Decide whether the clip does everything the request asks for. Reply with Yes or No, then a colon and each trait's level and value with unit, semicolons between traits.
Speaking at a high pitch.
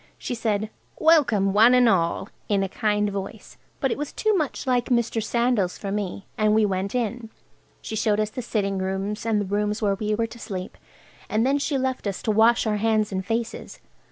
Yes: high, 215 Hz